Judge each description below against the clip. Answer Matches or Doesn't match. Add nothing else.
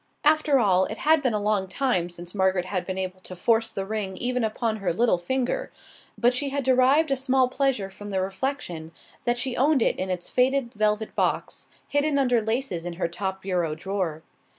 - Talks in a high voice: Matches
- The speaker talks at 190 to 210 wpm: Matches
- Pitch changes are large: Matches